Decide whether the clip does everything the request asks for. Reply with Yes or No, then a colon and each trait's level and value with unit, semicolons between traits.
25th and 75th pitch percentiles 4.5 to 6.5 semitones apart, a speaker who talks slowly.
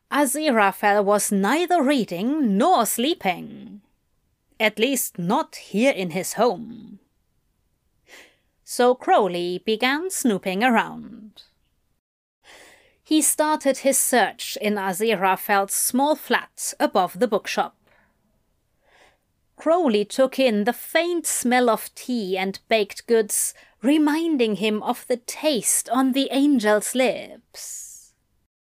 Yes: average, 5.0 semitones; slow, 105 wpm